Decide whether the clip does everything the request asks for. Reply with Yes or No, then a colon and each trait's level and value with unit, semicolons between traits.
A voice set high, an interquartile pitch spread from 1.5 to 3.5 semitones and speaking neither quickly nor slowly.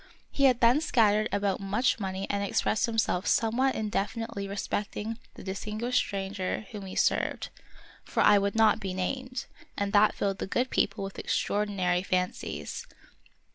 Yes: high, 205 Hz; narrow, 2.6 semitones; average, 155 wpm